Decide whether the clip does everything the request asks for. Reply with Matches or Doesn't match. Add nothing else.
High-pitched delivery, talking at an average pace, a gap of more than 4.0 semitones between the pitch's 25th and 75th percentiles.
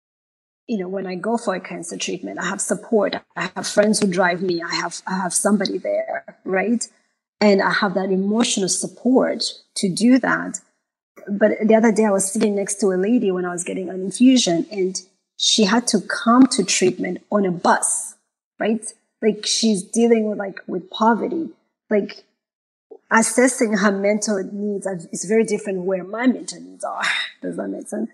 Doesn't match